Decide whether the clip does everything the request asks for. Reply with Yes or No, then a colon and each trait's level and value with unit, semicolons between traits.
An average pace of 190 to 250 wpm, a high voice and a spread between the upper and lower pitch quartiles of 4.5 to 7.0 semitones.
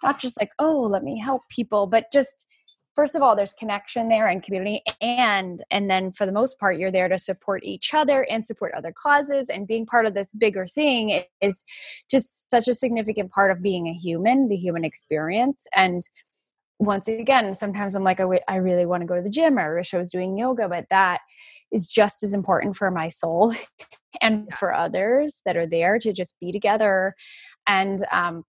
Yes: fast, 205 wpm; high, 205 Hz; average, 4.8 semitones